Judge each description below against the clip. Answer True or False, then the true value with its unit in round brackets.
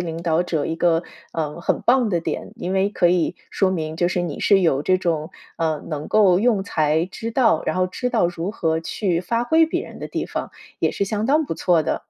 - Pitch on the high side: False (175 Hz)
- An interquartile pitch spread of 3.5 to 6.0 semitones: True (3.9 semitones)